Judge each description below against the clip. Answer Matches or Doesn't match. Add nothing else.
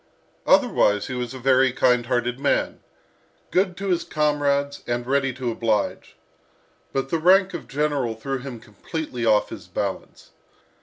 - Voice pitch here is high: Doesn't match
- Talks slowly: Doesn't match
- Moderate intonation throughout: Matches